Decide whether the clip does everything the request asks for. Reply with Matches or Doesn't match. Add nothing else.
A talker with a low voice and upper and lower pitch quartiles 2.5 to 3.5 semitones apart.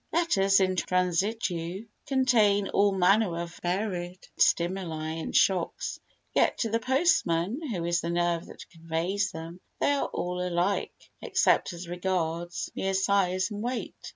Doesn't match